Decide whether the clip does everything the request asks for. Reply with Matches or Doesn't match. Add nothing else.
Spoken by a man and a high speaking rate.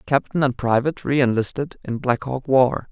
Doesn't match